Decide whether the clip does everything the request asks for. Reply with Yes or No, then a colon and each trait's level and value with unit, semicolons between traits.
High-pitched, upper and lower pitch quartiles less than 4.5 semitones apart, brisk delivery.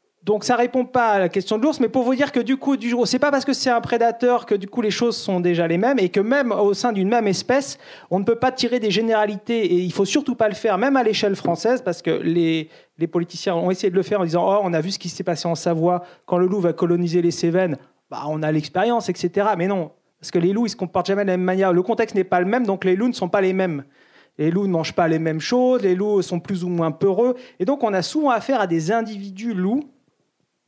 No: high, 200 Hz; average, 5.0 semitones; fast, 295 wpm